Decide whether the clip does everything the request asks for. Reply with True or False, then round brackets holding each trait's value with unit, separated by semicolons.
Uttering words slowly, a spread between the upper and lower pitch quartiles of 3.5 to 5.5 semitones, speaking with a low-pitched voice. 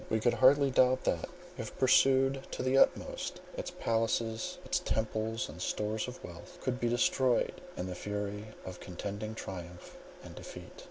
False (160 wpm; 3.9 semitones; 110 Hz)